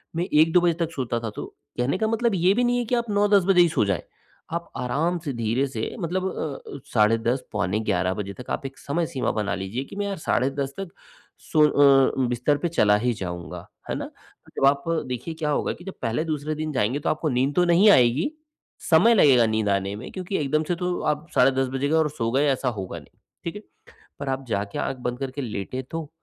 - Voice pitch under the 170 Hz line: Yes, medium, 140 Hz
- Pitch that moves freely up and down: Yes, wide, 6.2 semitones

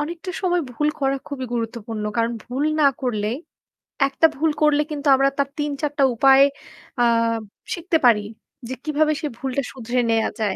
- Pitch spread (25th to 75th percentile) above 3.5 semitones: Yes, average, 4.1 semitones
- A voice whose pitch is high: Yes, very high, 275 Hz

